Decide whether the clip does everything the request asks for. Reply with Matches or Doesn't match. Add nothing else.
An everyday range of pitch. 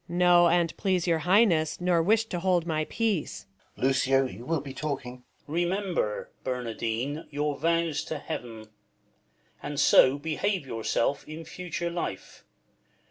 Matches